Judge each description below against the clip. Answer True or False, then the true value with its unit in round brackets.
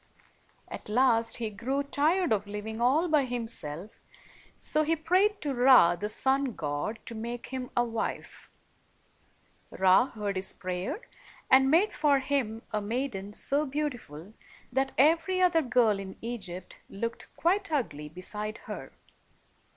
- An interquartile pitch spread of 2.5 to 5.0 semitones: False (5.4 semitones)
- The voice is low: False (240 Hz)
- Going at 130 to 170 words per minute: True (140 wpm)